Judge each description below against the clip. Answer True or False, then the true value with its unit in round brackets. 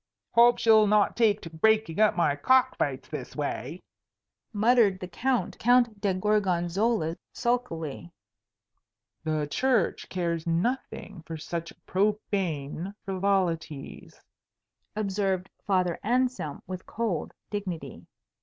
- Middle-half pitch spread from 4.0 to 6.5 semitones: True (4.4 semitones)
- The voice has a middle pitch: False (195 Hz)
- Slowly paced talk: True (105 wpm)